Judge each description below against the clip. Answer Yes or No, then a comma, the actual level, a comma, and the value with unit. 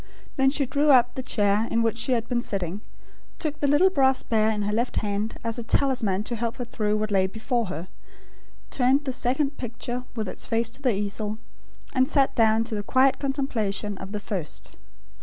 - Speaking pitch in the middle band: No, high, 230 Hz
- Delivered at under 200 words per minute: No, fast, 205 wpm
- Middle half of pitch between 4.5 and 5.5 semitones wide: No, average, 3.9 semitones